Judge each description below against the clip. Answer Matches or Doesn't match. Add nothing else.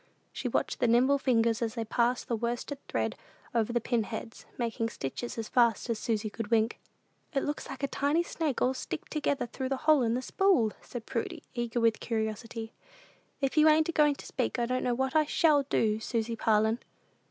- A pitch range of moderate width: Matches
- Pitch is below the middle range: Doesn't match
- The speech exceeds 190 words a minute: Matches